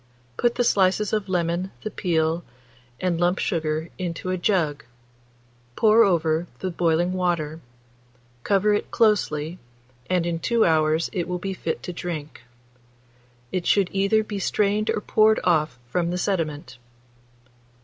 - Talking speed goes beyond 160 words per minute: No, average, 140 wpm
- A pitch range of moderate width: Yes, average, 3.4 semitones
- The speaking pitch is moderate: Yes, medium, 180 Hz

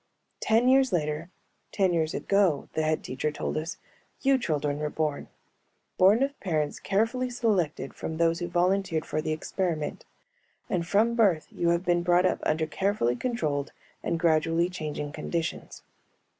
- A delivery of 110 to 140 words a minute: No, average, 155 wpm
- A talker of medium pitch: Yes, medium, 170 Hz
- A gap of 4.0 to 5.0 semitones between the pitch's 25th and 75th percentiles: Yes, average, 4.3 semitones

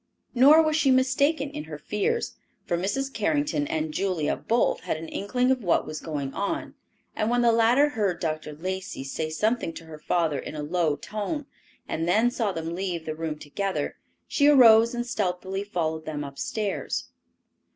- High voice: Yes, high, 200 Hz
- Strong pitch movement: Yes, wide, 8.0 semitones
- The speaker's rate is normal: Yes, average, 175 wpm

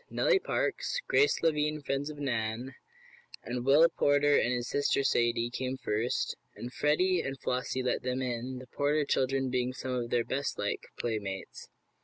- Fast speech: No, average, 160 wpm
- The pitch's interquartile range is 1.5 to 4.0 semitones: Yes, average, 2.9 semitones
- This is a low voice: Yes, low, 130 Hz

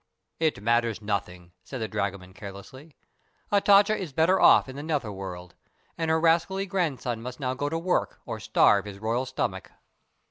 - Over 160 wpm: Yes, average, 170 wpm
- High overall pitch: No, low, 130 Hz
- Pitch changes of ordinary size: No, wide, 8.0 semitones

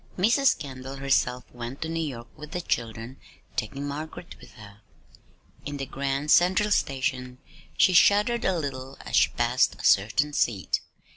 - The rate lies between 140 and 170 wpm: Yes, average, 155 wpm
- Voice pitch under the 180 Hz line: Yes, medium, 140 Hz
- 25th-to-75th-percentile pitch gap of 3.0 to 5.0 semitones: Yes, average, 4.6 semitones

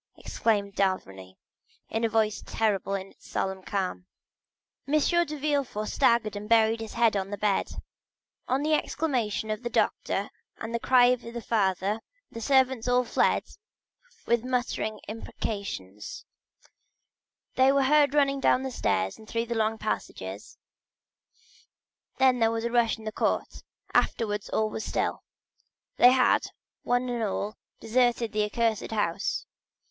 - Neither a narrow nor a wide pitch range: Yes, average, 3.2 semitones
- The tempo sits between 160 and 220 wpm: No, average, 150 wpm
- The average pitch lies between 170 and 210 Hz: No, high, 225 Hz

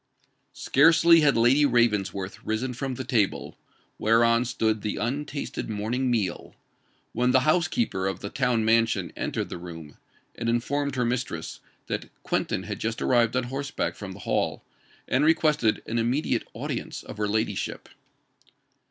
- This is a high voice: No, low, 120 Hz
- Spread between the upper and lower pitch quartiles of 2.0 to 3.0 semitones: No, average, 3.7 semitones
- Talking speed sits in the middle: Yes, average, 145 wpm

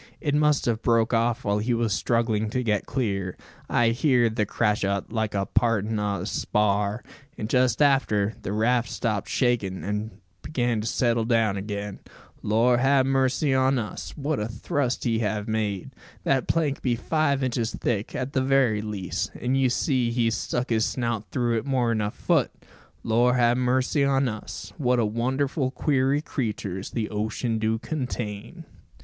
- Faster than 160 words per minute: Yes, average, 170 wpm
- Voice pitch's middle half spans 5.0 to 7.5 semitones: No, average, 3.4 semitones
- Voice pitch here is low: Yes, low, 115 Hz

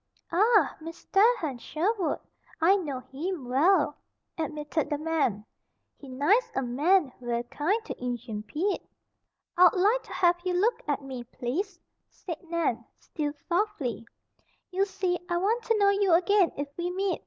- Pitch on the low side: No, very high, 335 Hz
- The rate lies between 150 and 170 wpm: Yes, average, 155 wpm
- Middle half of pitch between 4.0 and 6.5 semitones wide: Yes, wide, 5.8 semitones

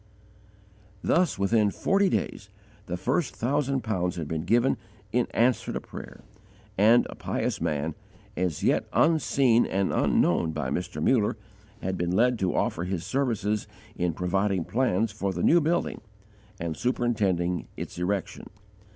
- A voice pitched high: No, low, 100 Hz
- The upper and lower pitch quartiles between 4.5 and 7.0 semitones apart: Yes, wide, 5.6 semitones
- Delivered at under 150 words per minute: Yes, average, 140 wpm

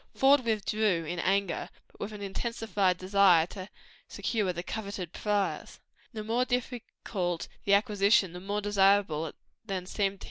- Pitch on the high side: Yes, high, 200 Hz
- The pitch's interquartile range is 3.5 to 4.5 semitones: No, average, 2.7 semitones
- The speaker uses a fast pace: No, average, 140 wpm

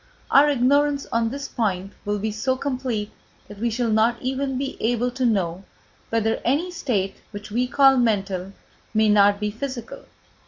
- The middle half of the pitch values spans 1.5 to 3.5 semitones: No, average, 4.1 semitones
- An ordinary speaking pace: Yes, average, 165 wpm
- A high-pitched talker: Yes, high, 230 Hz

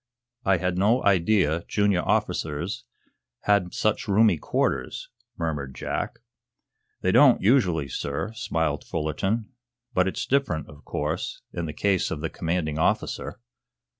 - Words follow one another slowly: Yes, slow, 130 wpm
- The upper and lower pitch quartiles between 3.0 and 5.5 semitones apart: Yes, average, 4.9 semitones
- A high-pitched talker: No, very low, 90 Hz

